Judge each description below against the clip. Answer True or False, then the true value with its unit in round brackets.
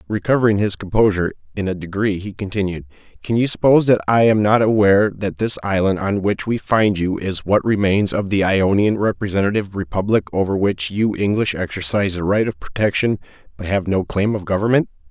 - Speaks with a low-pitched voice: True (100 Hz)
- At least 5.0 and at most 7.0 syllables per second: True (5.8 syllables/s)